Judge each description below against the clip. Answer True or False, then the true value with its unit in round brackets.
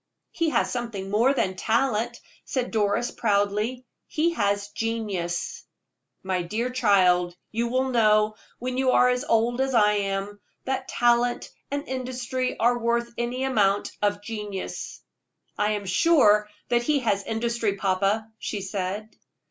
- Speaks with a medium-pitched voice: False (225 Hz)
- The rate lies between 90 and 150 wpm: True (140 wpm)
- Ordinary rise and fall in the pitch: True (3.5 semitones)